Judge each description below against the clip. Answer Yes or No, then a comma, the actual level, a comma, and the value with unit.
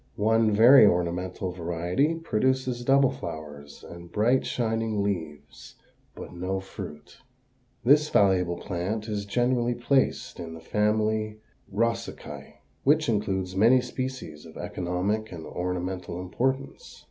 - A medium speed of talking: No, slow, 115 wpm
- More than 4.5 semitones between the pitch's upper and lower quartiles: Yes, average, 5.3 semitones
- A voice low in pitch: Yes, low, 105 Hz